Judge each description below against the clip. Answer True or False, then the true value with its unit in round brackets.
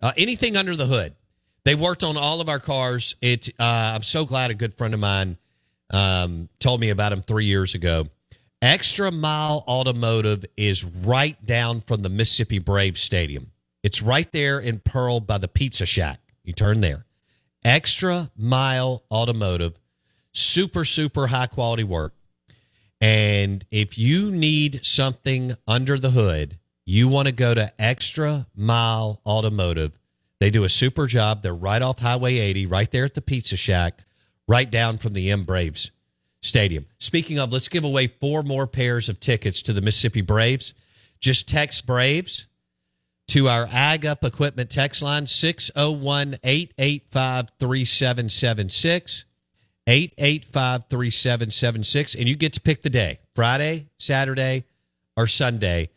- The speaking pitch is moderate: False (120 Hz)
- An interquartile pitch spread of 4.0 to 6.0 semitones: True (4.9 semitones)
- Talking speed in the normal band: True (150 wpm)